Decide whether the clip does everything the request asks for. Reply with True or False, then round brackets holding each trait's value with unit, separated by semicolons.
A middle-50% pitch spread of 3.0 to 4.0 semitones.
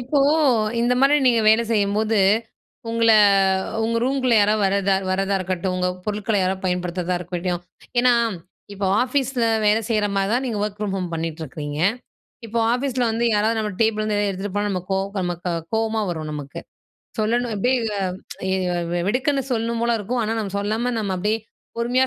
True (3.7 semitones)